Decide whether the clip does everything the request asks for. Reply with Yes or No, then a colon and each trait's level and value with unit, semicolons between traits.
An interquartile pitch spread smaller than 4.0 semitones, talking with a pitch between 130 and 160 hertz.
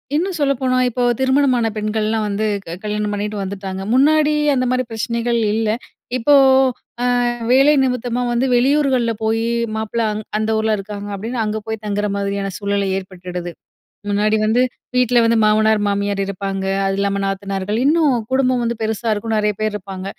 No: average, 3.5 semitones; high, 220 Hz